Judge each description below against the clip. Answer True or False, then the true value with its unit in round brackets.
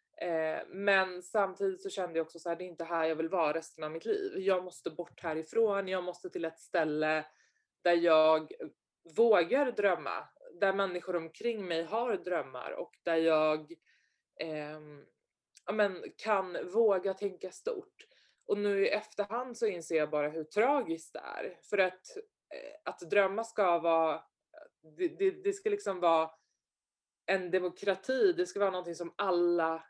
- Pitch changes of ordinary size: True (4.4 semitones)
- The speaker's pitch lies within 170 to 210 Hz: True (185 Hz)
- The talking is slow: False (160 wpm)